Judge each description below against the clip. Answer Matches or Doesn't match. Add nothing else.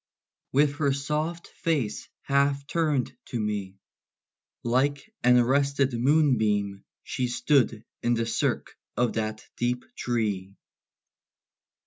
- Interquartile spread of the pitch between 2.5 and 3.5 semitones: Doesn't match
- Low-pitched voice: Matches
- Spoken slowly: Matches